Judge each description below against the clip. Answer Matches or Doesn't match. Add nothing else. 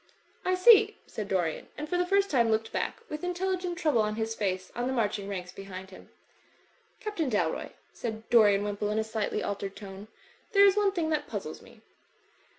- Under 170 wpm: Doesn't match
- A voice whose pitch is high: Matches